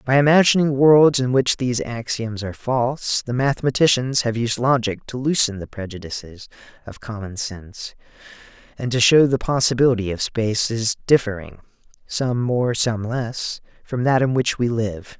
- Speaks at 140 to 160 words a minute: Yes, average, 145 wpm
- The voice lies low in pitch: Yes, low, 120 Hz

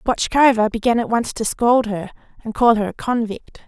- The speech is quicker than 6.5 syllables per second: No, 5.1 syllables/s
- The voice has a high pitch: Yes, high, 230 Hz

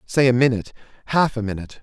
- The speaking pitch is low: Yes, low, 120 Hz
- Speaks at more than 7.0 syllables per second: Yes, 7.5 syllables/s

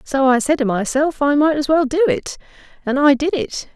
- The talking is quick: Yes, fast, 225 wpm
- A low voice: No, very high, 280 Hz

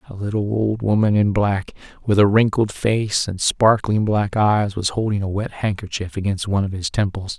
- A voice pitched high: No, low, 100 Hz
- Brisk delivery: No, average, 195 wpm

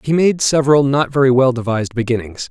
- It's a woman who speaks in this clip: No, male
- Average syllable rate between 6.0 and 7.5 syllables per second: Yes, 6.2 syllables/s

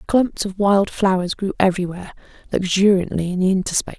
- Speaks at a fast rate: No, average, 150 wpm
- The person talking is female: Yes, female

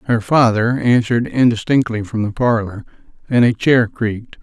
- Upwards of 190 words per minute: No, average, 150 wpm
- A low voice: Yes, low, 115 Hz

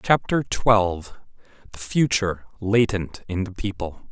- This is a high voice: No, low, 100 Hz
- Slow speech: Yes, slow, 100 wpm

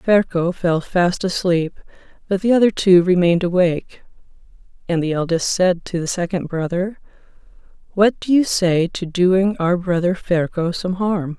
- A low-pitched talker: No, medium, 180 Hz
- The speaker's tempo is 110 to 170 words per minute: Yes, average, 155 wpm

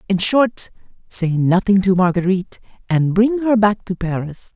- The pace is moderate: Yes, average, 160 wpm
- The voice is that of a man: No, female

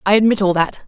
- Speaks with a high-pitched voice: Yes, high, 200 Hz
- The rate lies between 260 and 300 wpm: Yes, fast, 275 wpm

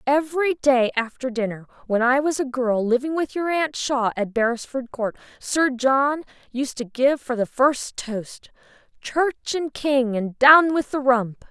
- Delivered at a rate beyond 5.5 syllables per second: No, 4.2 syllables/s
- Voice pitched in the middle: No, very high, 260 Hz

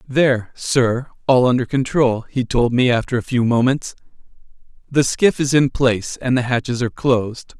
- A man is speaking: Yes, male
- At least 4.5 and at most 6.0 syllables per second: Yes, 5.0 syllables/s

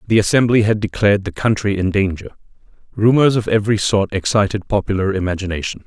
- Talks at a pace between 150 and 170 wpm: Yes, average, 155 wpm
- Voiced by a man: Yes, male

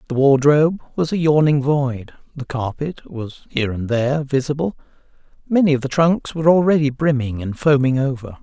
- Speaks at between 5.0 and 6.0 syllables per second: Yes, 5.4 syllables/s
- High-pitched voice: No, medium, 140 Hz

